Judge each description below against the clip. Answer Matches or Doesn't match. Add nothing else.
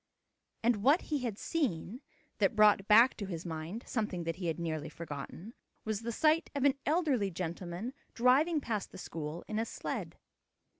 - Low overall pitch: Doesn't match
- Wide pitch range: Matches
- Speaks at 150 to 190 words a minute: Matches